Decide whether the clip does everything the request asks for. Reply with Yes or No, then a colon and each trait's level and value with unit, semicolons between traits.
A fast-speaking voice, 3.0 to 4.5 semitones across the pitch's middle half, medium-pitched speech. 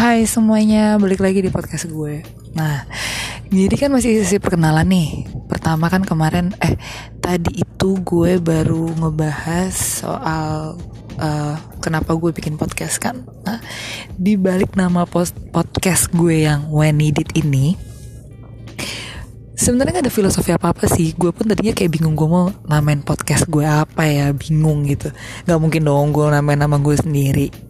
Yes: fast, 145 wpm; average, 3.7 semitones; medium, 160 Hz